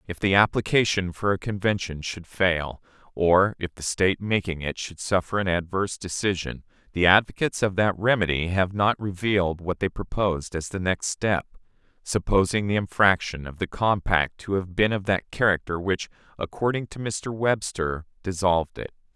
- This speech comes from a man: Yes, male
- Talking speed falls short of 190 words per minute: Yes, average, 165 wpm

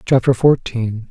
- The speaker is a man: Yes, male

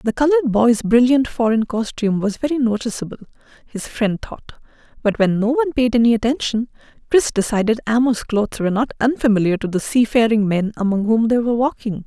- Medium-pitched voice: No, high, 230 Hz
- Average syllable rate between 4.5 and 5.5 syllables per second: No, 5.9 syllables/s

